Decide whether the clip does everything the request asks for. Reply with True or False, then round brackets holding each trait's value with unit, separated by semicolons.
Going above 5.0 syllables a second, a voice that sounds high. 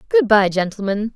True (5.2 syllables/s; 220 Hz)